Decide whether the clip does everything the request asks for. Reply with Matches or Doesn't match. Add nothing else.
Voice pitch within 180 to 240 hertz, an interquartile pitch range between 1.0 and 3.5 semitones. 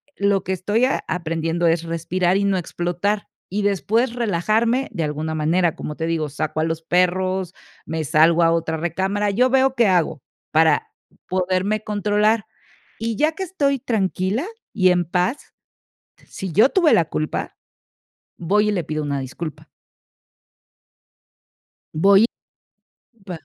Doesn't match